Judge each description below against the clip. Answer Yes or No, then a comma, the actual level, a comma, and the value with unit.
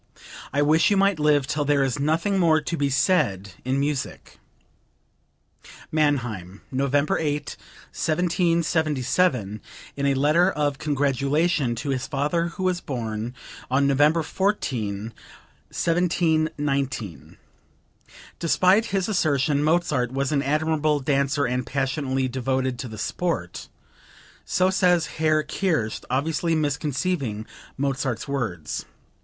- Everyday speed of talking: No, slow, 115 wpm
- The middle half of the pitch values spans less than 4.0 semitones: Yes, average, 3.6 semitones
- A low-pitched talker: No, medium, 145 Hz